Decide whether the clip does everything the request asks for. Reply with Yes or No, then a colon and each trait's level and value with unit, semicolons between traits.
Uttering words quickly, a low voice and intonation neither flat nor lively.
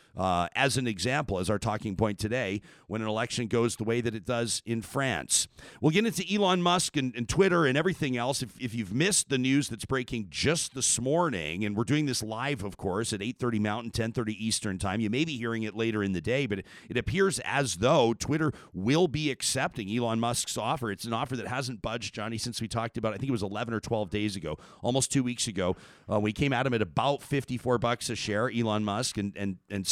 Yes: fast, 240 wpm; low, 120 Hz; average, 4.0 semitones